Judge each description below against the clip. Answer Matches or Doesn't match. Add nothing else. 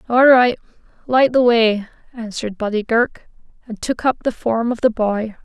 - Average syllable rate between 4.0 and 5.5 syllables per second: Matches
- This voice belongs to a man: Doesn't match